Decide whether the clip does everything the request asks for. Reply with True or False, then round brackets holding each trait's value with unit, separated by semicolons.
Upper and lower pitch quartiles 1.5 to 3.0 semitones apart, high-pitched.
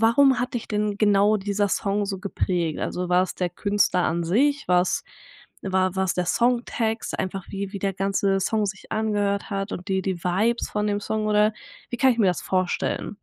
True (2.4 semitones; 200 Hz)